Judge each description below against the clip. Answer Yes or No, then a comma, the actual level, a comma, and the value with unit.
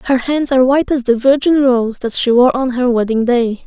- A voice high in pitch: Yes, very high, 250 Hz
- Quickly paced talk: Yes, fast, 245 wpm